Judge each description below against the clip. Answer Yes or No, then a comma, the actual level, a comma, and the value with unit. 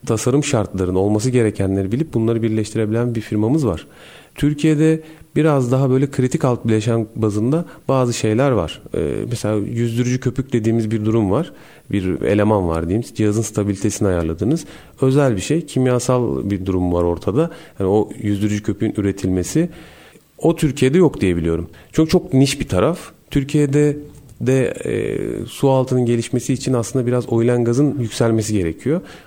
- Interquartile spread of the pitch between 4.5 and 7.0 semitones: Yes, average, 5.1 semitones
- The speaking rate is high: Yes, fast, 145 wpm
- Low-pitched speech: Yes, low, 120 Hz